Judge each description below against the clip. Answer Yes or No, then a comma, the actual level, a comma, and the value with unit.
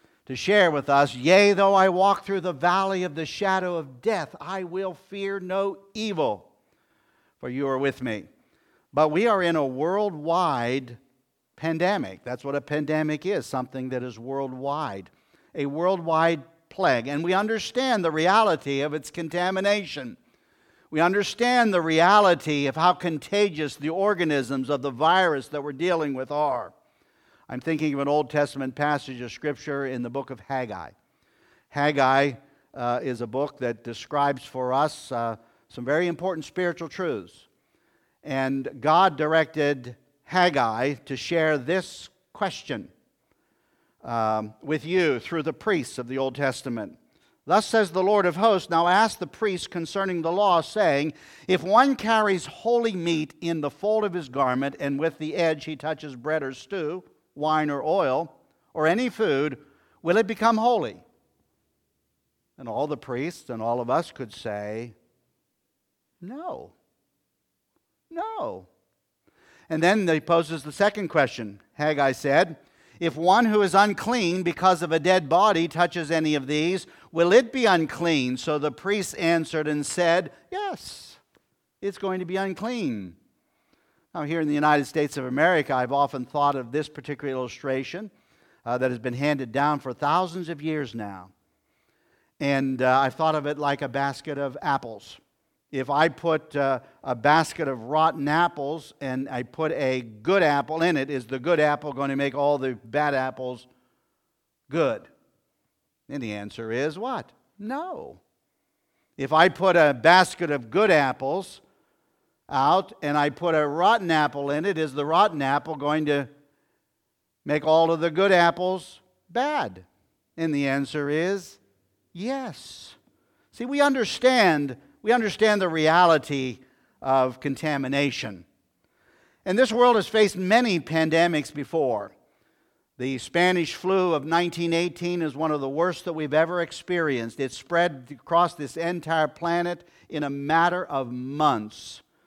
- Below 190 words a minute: Yes, average, 150 wpm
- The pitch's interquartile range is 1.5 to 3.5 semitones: No, average, 4.8 semitones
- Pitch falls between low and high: Yes, medium, 155 Hz